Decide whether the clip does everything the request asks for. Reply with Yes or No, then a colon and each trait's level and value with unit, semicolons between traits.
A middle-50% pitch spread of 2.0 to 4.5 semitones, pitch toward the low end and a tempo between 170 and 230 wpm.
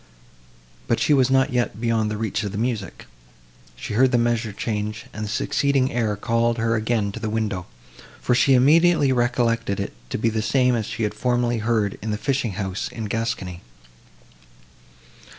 Yes: narrow, 2.5 semitones; low, 115 Hz; average, 175 wpm